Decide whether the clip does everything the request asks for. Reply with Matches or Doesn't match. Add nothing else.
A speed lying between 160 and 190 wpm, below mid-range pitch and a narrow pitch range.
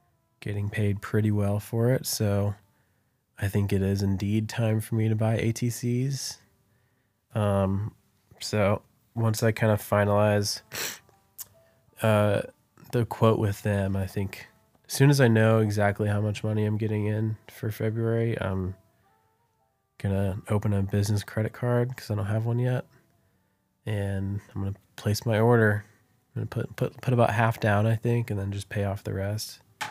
Matches